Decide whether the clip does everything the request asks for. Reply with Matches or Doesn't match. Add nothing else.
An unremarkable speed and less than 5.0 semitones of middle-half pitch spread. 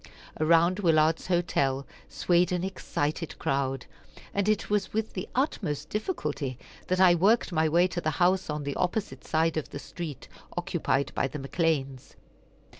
Matches